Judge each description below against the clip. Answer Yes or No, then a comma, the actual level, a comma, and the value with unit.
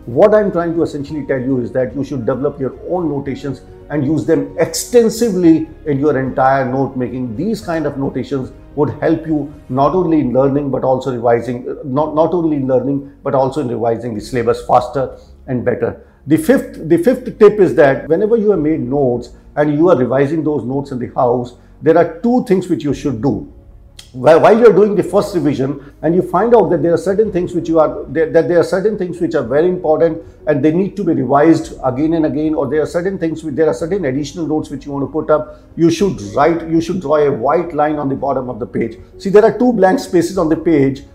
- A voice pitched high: No, medium, 150 Hz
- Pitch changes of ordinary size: Yes, average, 4.1 semitones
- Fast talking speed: Yes, fast, 230 wpm